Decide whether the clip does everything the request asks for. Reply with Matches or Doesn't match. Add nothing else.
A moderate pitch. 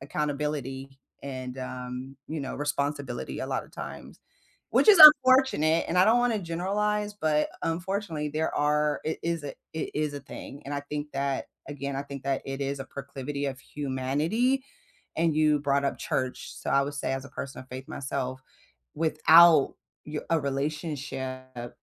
Matches